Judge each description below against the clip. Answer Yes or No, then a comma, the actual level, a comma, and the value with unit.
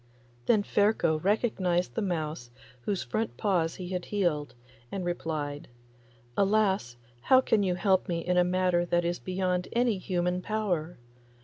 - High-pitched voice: No, medium, 180 Hz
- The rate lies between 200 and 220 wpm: No, average, 150 wpm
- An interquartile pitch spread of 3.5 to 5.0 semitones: No, average, 3.0 semitones